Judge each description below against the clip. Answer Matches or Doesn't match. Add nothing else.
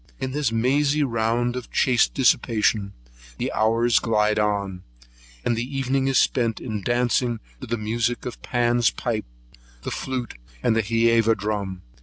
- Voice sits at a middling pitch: Doesn't match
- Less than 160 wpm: Matches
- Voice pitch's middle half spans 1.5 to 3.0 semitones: Matches